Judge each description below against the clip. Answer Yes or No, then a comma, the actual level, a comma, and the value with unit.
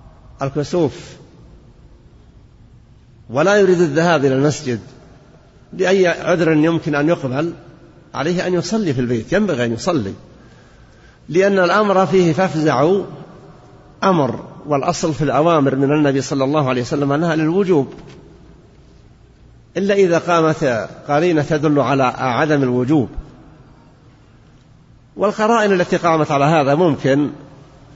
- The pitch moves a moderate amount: Yes, average, 4.3 semitones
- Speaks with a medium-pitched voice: Yes, medium, 155 Hz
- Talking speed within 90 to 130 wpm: Yes, average, 105 wpm